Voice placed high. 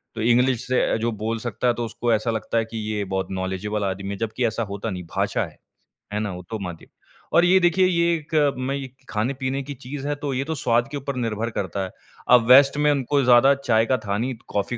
No: low, 120 Hz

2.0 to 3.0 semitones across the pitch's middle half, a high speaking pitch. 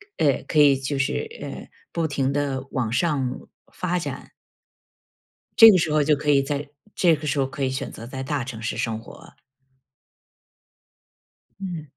No: narrow, 2.5 semitones; medium, 140 Hz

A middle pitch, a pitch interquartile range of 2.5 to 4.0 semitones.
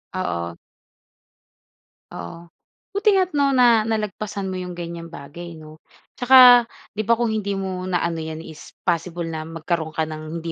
No: medium, 175 Hz; average, 4.9 semitones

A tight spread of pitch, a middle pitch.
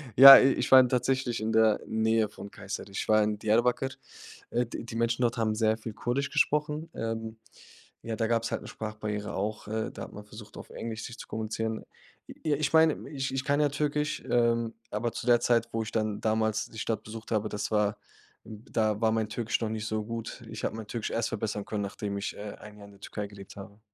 No: narrow, 1.9 semitones; low, 110 Hz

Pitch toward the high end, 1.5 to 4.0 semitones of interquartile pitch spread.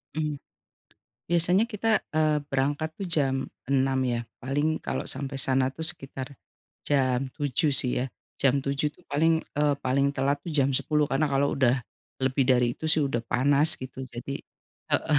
No: medium, 140 Hz; narrow, 2.5 semitones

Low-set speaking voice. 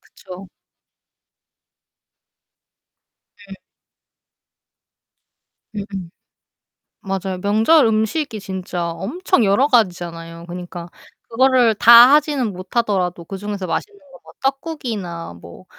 No: high, 200 Hz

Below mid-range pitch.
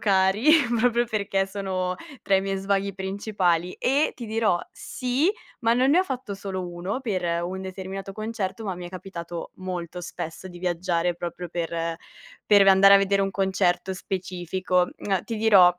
No: high, 190 Hz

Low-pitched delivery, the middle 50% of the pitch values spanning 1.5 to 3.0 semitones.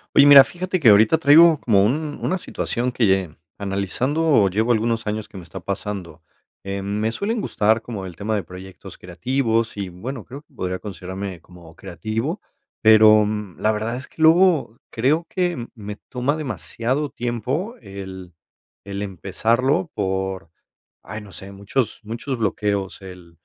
No: low, 110 Hz; average, 5.3 semitones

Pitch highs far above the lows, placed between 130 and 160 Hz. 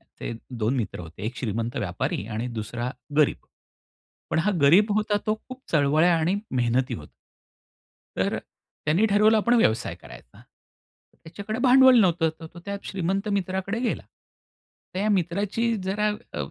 No: wide, 9.0 semitones; medium, 175 Hz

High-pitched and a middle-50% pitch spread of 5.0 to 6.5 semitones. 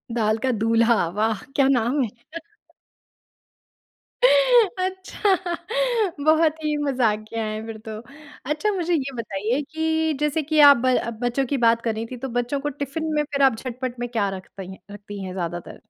Yes: very high, 255 Hz; wide, 5.5 semitones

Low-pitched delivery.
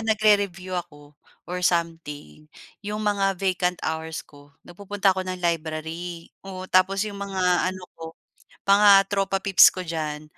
No: medium, 180 Hz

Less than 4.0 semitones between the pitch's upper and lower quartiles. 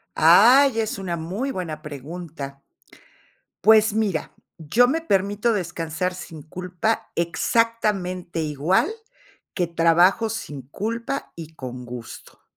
No: wide, 5.4 semitones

